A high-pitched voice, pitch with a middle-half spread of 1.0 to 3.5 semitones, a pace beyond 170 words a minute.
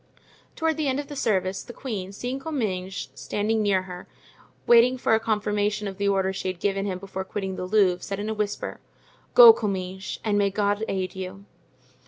Yes: high, 205 Hz; average, 2.7 semitones; average, 195 wpm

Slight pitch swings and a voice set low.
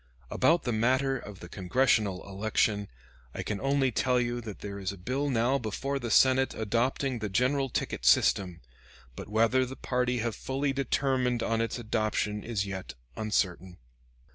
No: average, 4.0 semitones; low, 115 Hz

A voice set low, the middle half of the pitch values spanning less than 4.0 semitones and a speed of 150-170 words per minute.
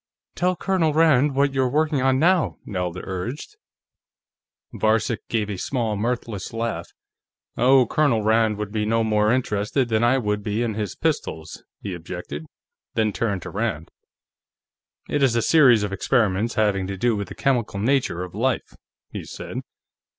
No: low, 115 Hz; average, 4.4 semitones; average, 160 wpm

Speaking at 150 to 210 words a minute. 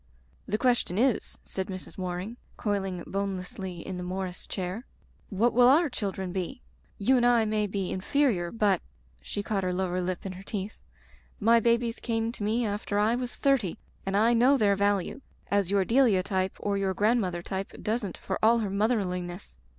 Yes: average, 190 wpm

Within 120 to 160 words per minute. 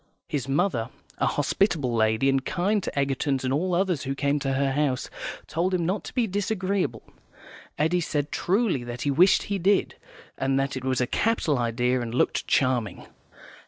No: average, 180 wpm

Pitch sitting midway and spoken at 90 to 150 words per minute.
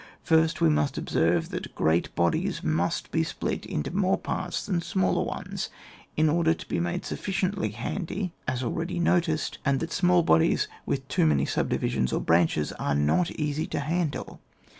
No: medium, 155 Hz; average, 165 wpm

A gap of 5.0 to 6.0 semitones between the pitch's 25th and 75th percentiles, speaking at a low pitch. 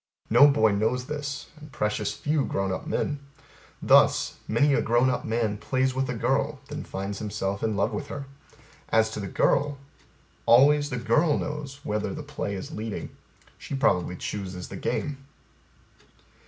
Yes: average, 5.3 semitones; low, 125 Hz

